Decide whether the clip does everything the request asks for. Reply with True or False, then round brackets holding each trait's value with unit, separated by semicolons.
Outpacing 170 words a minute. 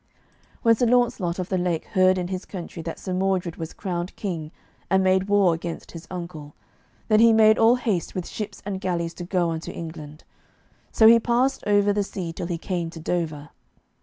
True (195 wpm)